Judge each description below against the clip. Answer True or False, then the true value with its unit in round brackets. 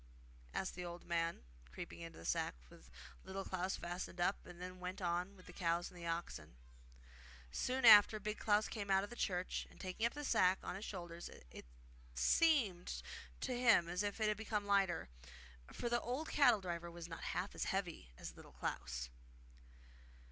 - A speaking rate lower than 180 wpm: False (185 wpm)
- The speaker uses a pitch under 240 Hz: True (185 Hz)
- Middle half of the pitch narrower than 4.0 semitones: True (3.4 semitones)